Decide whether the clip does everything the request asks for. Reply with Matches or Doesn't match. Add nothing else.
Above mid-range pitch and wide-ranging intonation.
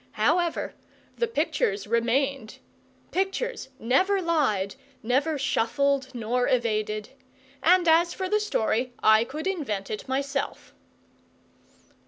Matches